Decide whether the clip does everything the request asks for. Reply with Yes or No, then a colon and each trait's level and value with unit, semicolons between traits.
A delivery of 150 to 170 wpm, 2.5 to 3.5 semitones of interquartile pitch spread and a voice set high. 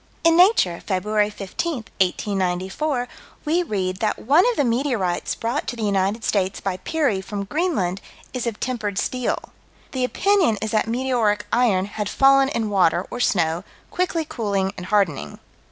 No: average, 155 wpm; wide, 5.4 semitones; high, 215 Hz